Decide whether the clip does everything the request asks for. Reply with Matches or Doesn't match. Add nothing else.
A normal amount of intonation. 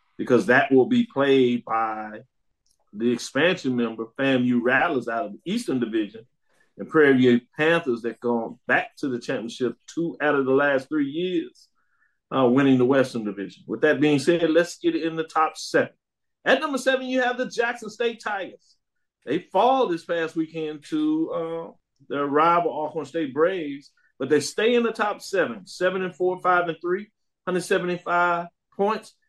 Doesn't match